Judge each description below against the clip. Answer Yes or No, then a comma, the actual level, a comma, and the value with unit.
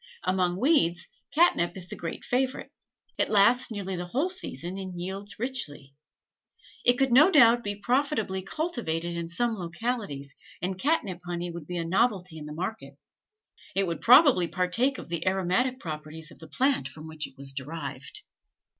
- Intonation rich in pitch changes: Yes, wide, 6.5 semitones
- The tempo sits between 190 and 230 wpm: No, average, 165 wpm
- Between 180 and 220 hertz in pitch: Yes, medium, 185 Hz